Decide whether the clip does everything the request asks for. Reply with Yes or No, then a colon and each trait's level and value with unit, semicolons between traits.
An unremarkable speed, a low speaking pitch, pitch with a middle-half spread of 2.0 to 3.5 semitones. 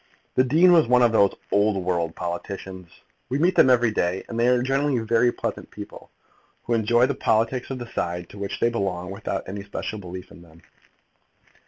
No: average, 190 wpm; low, 110 Hz; average, 5.2 semitones